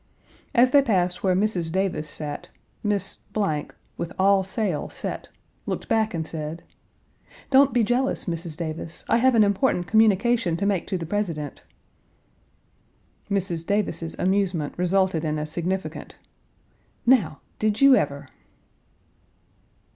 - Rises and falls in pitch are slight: No, average, 4.5 semitones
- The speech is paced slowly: Yes, slow, 125 wpm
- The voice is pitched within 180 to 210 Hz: Yes, high, 190 Hz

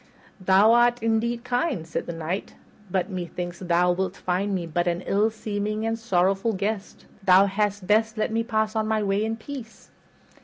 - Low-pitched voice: No, high, 205 Hz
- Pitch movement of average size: Yes, average, 3.3 semitones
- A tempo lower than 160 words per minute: No, average, 180 wpm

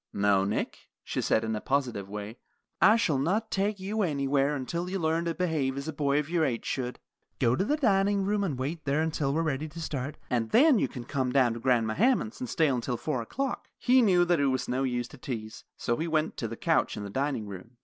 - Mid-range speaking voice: Yes, medium, 145 Hz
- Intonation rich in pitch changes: Yes, wide, 6.1 semitones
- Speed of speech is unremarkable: No, fast, 245 wpm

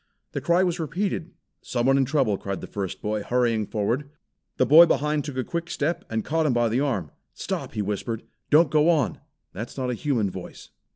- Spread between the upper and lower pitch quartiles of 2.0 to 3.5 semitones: No, wide, 5.6 semitones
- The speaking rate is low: No, fast, 205 wpm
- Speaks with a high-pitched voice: No, low, 130 Hz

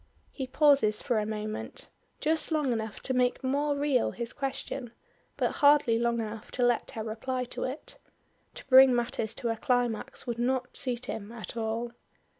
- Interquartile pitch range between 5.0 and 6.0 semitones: No, average, 2.8 semitones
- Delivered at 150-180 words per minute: Yes, average, 175 wpm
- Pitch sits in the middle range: No, high, 245 Hz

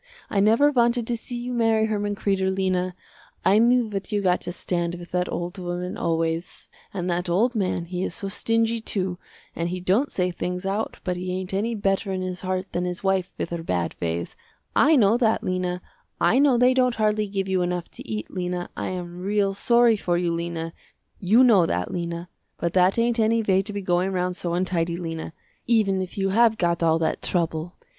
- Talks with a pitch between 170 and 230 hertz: Yes, medium, 185 Hz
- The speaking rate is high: Yes, fast, 210 wpm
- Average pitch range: Yes, average, 3.6 semitones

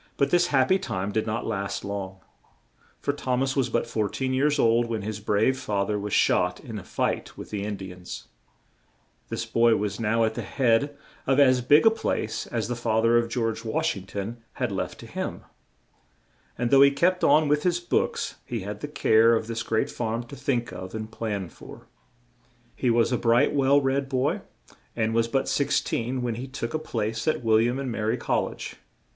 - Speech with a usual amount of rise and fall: Yes, average, 3.6 semitones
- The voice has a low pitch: Yes, low, 115 Hz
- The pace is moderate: No, fast, 215 wpm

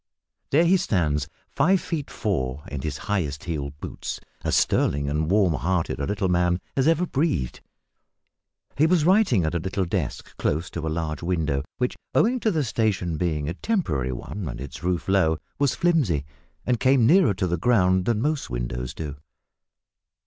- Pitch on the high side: No, very low, 90 Hz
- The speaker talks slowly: No, average, 175 wpm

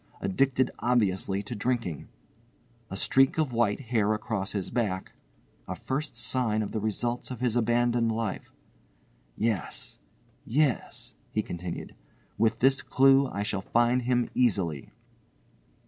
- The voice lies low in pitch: Yes, low, 115 Hz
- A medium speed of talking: No, slow, 125 wpm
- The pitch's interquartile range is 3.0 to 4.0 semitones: Yes, average, 3.7 semitones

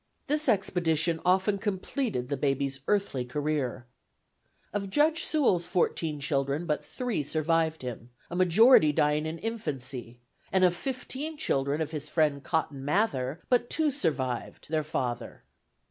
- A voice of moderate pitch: Yes, medium, 160 Hz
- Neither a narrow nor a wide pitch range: No, wide, 6.1 semitones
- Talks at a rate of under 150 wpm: Yes, slow, 135 wpm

